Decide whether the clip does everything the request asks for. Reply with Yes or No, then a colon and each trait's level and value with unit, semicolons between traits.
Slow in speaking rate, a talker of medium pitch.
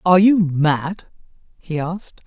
Yes: slow, 130 wpm; medium, 170 Hz